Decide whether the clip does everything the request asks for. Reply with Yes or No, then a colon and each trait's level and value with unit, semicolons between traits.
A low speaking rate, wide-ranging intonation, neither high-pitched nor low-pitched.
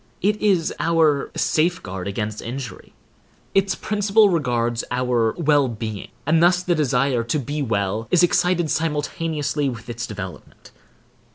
Yes: slow, 130 wpm; wide, 6.3 semitones; medium, 145 Hz